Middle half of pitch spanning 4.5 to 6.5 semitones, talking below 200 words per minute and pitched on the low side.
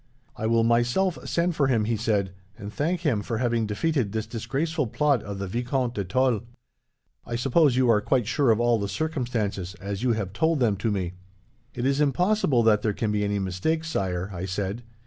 No: average, 4.9 semitones; fast, 205 wpm; low, 115 Hz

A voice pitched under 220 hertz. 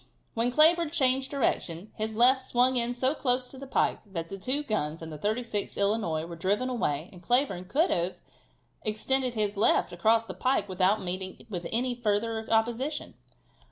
No: high, 225 Hz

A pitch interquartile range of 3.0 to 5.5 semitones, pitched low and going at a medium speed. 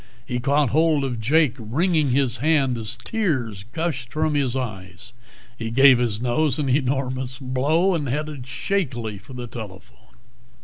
Yes: average, 4.1 semitones; low, 130 Hz; average, 150 wpm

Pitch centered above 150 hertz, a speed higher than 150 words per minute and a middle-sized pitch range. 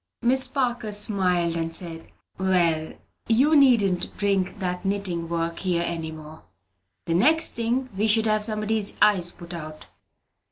No: high, 190 Hz; average, 145 wpm; average, 4.6 semitones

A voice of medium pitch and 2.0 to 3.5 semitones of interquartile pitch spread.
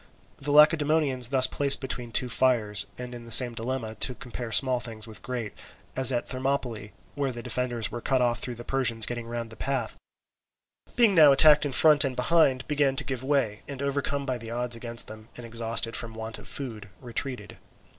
No: low, 125 Hz; average, 2.9 semitones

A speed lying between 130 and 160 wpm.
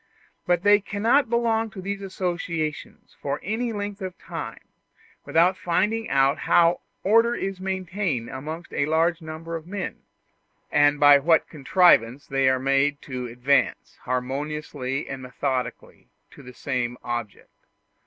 Yes: slow, 135 wpm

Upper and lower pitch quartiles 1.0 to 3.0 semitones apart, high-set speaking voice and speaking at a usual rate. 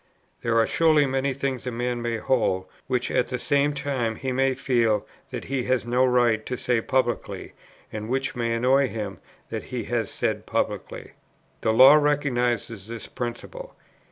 No: narrow, 2.5 semitones; low, 125 Hz; average, 175 wpm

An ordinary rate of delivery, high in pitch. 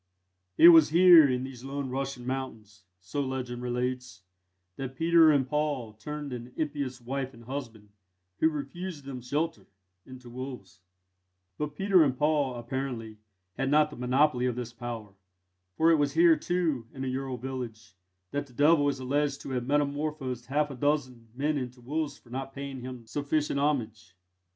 No: average, 165 wpm; low, 135 Hz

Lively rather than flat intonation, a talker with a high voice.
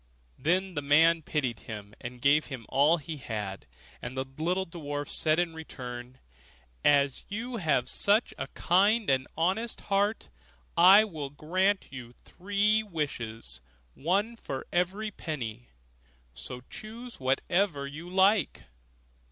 No: wide, 6.6 semitones; medium, 160 Hz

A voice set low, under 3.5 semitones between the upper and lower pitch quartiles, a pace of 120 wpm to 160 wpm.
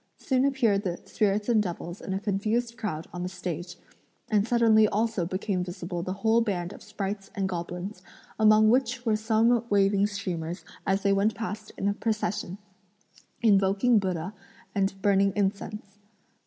No: high, 200 Hz; narrow, 2.6 semitones; average, 155 wpm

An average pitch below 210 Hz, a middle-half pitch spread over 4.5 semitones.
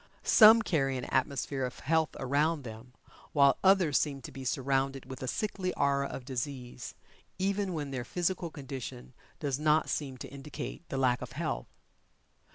No: medium, 140 Hz; average, 3.4 semitones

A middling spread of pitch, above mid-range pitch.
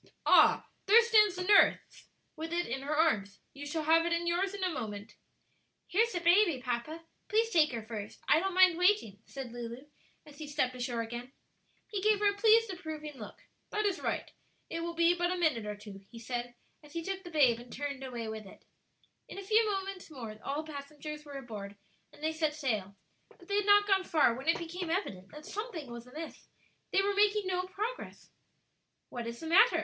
No: wide, 7.5 semitones; very high, 315 Hz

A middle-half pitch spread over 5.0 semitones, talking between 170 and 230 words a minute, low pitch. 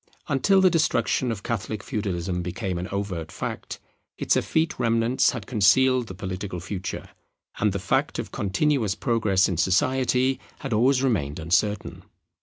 No: wide, 5.4 semitones; average, 145 wpm; low, 105 Hz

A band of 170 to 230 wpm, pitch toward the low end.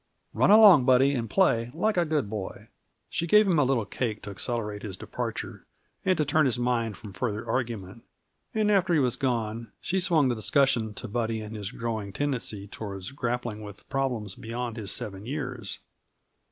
Yes: average, 180 wpm; low, 120 Hz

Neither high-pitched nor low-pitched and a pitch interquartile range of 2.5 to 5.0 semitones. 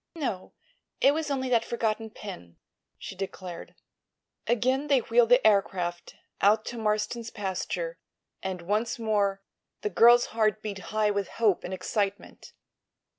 No: high, 215 Hz; average, 3.3 semitones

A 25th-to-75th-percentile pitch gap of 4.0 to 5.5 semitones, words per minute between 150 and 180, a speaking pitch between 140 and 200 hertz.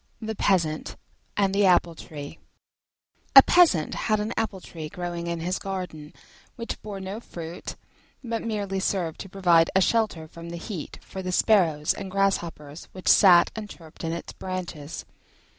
No: average, 3.2 semitones; average, 160 wpm; medium, 185 Hz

